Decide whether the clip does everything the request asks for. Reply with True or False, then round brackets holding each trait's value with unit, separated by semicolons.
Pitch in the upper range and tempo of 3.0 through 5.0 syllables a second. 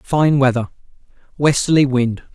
False (135 Hz; 4.7 syllables/s)